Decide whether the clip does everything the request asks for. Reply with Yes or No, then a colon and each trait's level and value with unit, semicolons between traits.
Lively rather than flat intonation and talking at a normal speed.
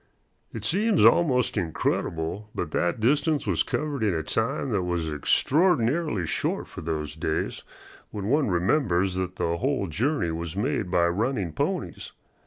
Yes: wide, 8.2 semitones; average, 150 wpm